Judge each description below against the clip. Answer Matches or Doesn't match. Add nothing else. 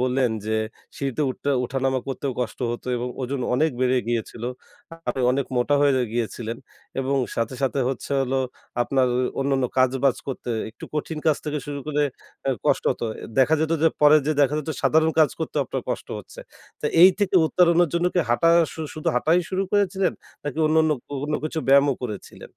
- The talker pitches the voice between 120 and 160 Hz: Matches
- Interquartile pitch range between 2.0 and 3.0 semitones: Doesn't match